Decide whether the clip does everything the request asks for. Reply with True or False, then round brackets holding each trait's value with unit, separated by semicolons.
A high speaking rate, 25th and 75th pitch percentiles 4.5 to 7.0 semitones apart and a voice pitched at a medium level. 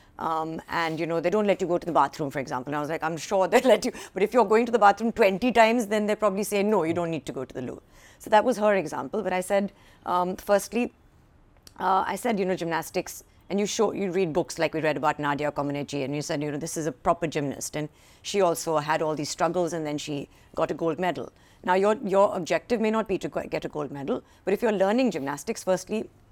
True (260 wpm; 4.8 semitones; 175 Hz)